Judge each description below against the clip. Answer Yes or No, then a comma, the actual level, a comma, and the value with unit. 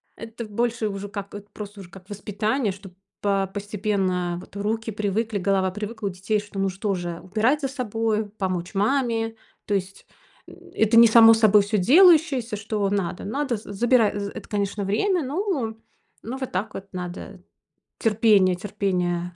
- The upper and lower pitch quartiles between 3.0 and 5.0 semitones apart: No, narrow, 2.6 semitones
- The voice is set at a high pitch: Yes, high, 205 Hz